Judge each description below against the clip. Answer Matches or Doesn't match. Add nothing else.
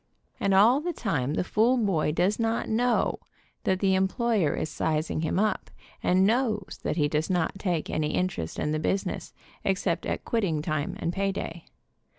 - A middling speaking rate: Matches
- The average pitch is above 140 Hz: Matches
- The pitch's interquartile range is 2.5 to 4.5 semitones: Doesn't match